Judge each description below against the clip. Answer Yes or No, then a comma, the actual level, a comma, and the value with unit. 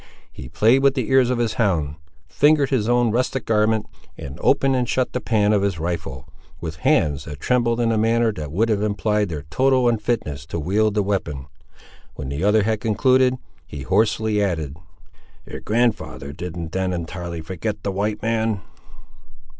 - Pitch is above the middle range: No, low, 105 Hz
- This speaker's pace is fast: No, average, 175 wpm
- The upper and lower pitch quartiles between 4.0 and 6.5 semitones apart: Yes, wide, 5.6 semitones